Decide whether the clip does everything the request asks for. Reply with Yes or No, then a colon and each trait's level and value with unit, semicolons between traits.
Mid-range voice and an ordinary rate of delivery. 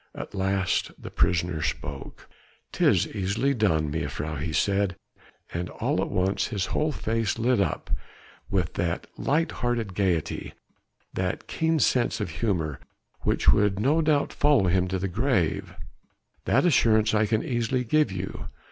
No: low, 100 Hz; average, 145 wpm